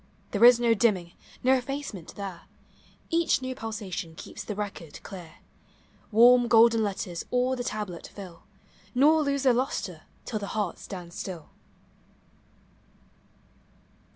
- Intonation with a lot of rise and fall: No, average, 4.9 semitones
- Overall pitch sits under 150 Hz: No, high, 220 Hz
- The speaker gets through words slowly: Yes, slow, 125 wpm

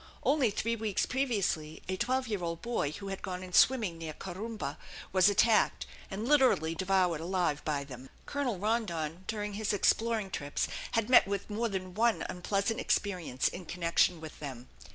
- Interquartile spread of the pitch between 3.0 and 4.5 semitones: No, average, 5.0 semitones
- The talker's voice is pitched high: Yes, high, 195 Hz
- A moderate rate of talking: Yes, average, 170 wpm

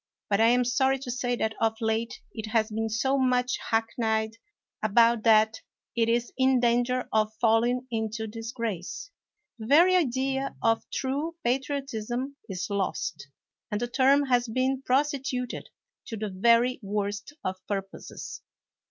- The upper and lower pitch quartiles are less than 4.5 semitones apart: Yes, average, 2.9 semitones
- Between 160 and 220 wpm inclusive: No, average, 150 wpm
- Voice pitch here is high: Yes, high, 235 Hz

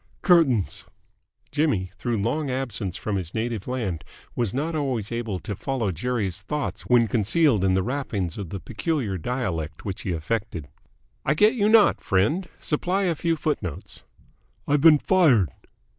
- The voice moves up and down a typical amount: No, wide, 7.6 semitones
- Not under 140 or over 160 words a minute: Yes, average, 155 wpm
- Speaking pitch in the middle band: No, low, 120 Hz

